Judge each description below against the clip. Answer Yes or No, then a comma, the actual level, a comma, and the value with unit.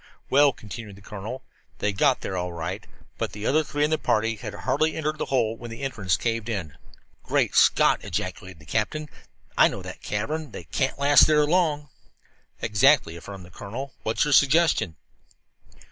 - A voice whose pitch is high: No, low, 115 Hz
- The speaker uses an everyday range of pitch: No, wide, 6.5 semitones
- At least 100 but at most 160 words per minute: No, average, 180 wpm